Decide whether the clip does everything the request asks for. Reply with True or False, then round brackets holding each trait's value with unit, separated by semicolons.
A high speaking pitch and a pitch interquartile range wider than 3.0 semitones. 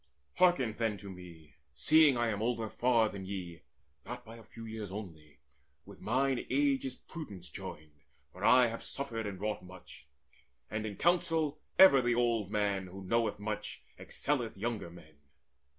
False (110 Hz; 4.5 semitones)